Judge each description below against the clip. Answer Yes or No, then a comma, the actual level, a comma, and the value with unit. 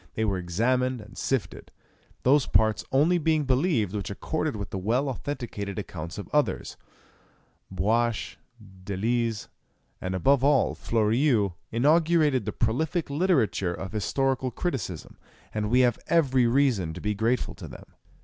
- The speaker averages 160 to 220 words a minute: No, average, 140 wpm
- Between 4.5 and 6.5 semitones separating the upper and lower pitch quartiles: Yes, average, 5.2 semitones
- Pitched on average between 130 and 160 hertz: No, low, 120 Hz